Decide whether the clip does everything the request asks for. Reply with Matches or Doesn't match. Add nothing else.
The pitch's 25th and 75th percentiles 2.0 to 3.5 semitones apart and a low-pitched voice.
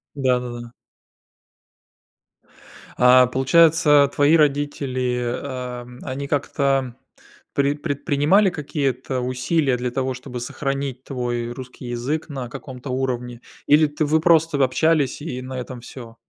Matches